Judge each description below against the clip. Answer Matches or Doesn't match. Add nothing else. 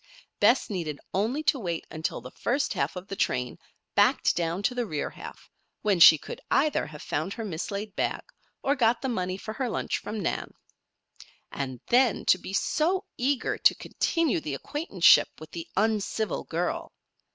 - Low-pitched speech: Doesn't match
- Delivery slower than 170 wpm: Doesn't match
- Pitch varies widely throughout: Matches